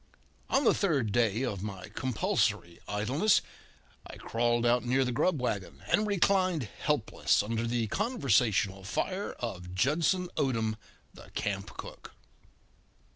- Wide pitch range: Yes, wide, 7.8 semitones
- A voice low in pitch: Yes, low, 120 Hz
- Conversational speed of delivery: No, slow, 130 wpm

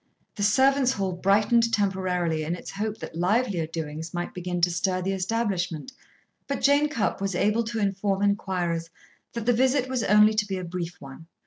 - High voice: Yes, high, 195 Hz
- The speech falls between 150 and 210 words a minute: Yes, average, 185 wpm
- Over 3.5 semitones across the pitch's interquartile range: Yes, average, 4.3 semitones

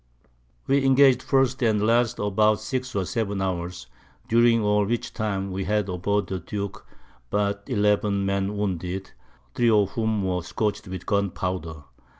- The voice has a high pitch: No, low, 105 Hz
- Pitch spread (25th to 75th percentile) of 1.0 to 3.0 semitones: Yes, average, 2.7 semitones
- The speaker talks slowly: No, average, 150 wpm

